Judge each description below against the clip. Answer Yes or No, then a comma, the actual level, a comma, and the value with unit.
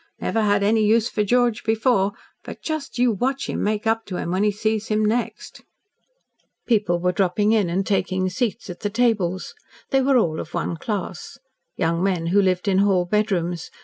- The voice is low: No, high, 205 Hz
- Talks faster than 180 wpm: Yes, average, 190 wpm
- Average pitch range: Yes, average, 3.4 semitones